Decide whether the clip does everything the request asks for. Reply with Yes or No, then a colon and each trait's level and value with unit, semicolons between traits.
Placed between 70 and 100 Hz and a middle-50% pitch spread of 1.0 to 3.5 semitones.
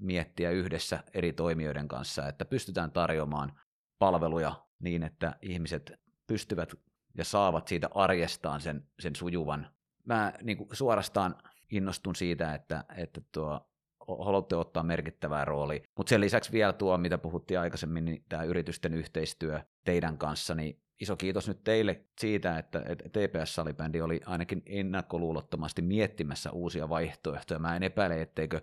Yes: very low, 85 Hz; average, 2.9 semitones